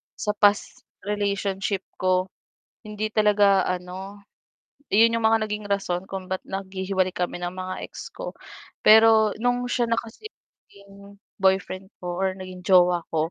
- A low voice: No, high, 195 Hz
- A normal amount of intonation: No, narrow, 2.2 semitones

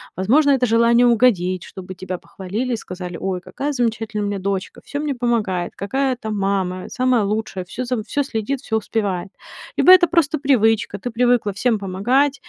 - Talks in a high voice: Yes, high, 225 Hz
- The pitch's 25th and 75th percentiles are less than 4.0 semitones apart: No, average, 4.6 semitones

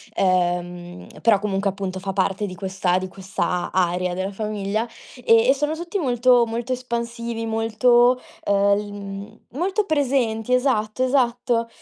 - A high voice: Yes, high, 220 Hz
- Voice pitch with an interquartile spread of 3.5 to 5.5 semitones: Yes, average, 4.2 semitones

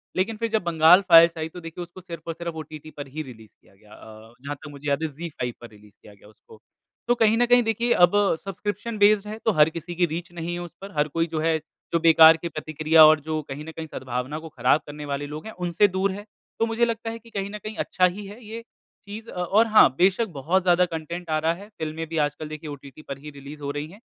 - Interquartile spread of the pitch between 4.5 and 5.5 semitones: Yes, average, 4.8 semitones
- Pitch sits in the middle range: Yes, medium, 165 Hz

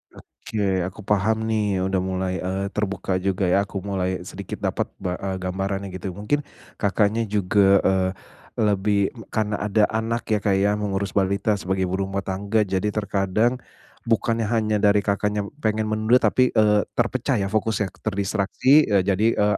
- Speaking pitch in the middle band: No, low, 100 Hz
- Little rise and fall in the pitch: Yes, narrow, 2.0 semitones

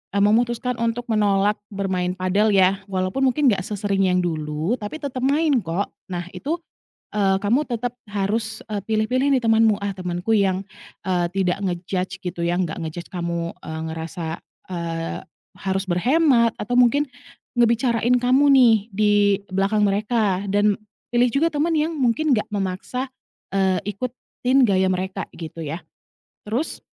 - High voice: Yes, high, 205 Hz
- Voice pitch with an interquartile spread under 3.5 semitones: No, average, 4.6 semitones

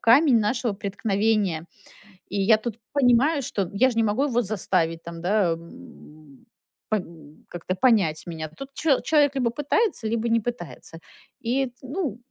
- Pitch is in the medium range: No, high, 220 Hz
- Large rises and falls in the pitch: Yes, wide, 5.9 semitones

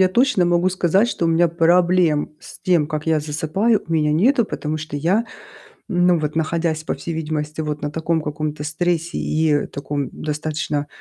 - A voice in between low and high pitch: Yes, medium, 160 Hz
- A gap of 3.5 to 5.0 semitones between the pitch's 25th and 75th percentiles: No, narrow, 2.6 semitones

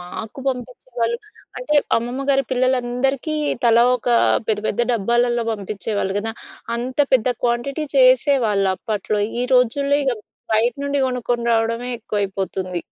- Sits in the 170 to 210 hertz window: No, high, 240 Hz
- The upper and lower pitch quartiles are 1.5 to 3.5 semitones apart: Yes, average, 2.9 semitones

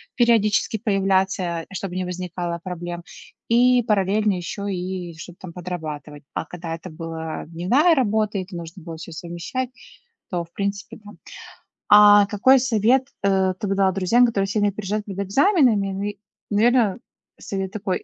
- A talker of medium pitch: No, high, 195 Hz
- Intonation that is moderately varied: Yes, average, 3.2 semitones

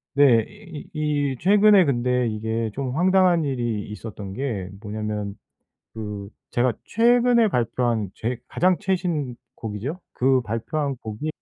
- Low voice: Yes, low, 125 Hz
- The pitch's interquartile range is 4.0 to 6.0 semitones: No, wide, 7.1 semitones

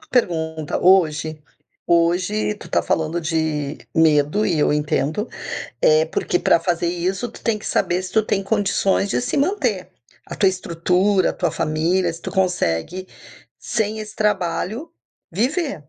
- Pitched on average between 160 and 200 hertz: Yes, medium, 185 Hz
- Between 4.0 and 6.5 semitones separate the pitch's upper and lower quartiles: Yes, average, 4.5 semitones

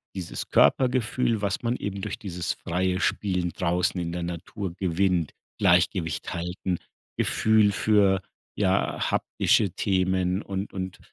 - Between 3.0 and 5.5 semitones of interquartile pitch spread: No, narrow, 2.4 semitones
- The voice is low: Yes, very low, 95 Hz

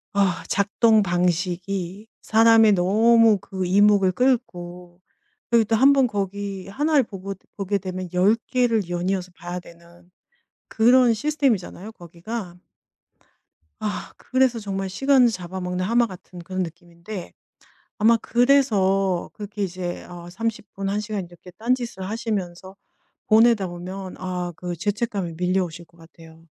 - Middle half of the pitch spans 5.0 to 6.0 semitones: No, average, 3.9 semitones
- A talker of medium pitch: No, high, 195 Hz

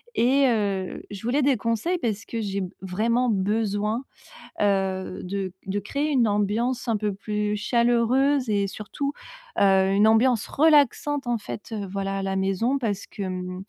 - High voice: Yes, high, 210 Hz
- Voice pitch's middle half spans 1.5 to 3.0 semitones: No, average, 3.7 semitones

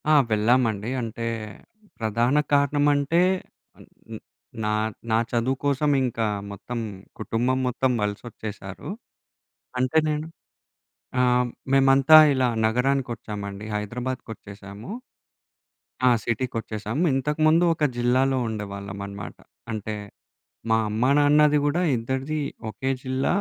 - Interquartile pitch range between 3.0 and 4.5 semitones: Yes, average, 4.0 semitones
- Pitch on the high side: No, low, 125 Hz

